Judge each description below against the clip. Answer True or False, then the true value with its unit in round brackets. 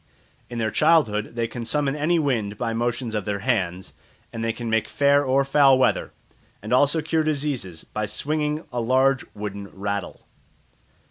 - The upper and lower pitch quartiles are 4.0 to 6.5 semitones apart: True (5.1 semitones)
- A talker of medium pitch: False (120 Hz)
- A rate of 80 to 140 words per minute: False (170 wpm)